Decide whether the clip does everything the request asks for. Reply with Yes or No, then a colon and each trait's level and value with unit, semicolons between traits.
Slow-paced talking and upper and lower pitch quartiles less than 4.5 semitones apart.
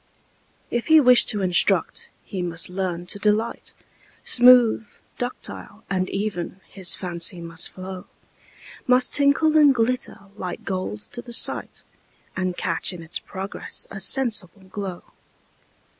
No: slow, 130 wpm; average, 4.9 semitones